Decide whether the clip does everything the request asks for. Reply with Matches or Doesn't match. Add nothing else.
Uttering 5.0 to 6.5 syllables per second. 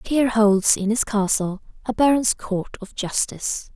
Doesn't match